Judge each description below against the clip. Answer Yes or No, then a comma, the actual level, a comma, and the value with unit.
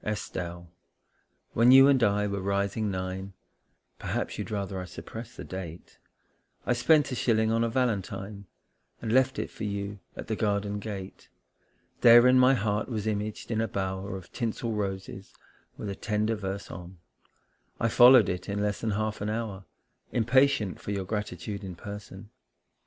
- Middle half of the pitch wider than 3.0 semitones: No, average, 2.7 semitones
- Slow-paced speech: No, average, 165 wpm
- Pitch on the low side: Yes, low, 105 Hz